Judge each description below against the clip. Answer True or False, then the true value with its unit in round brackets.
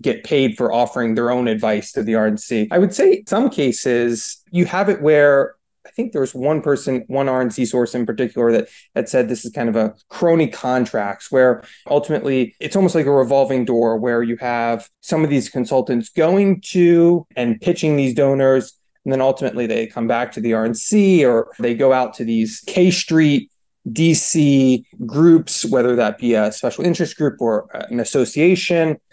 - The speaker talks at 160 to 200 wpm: True (185 wpm)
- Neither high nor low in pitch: False (130 Hz)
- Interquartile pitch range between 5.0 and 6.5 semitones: True (5.3 semitones)